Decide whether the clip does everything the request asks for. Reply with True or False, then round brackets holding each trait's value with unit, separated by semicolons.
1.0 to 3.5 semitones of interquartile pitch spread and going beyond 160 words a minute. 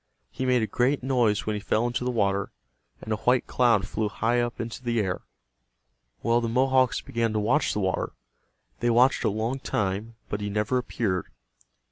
True (3.0 semitones; 190 wpm)